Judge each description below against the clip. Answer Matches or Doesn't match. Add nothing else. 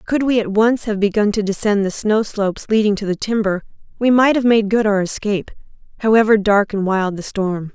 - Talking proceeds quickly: Matches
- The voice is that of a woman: Matches